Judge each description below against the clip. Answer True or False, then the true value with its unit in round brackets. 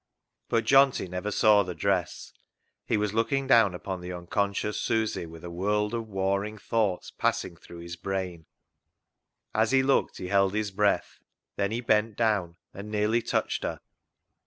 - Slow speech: False (160 wpm)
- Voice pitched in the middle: False (100 Hz)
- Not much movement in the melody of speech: False (3.1 semitones)